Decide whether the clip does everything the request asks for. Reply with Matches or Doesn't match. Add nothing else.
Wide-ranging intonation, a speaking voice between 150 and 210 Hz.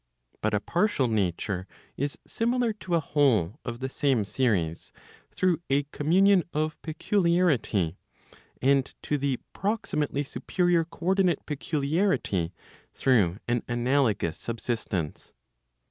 Doesn't match